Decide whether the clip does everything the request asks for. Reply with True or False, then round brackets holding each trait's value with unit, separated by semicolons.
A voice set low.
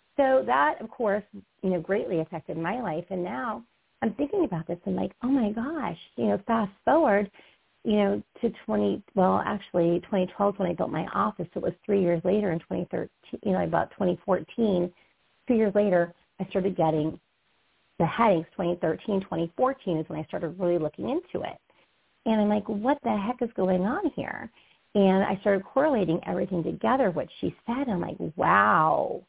False (195 Hz)